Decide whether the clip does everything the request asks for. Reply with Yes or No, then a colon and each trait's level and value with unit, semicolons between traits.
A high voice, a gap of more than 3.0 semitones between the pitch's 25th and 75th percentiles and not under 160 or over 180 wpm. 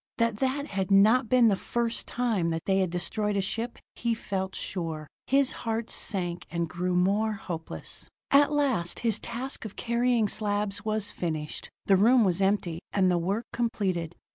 Yes: high, 205 Hz; average, 4.3 semitones; average, 170 wpm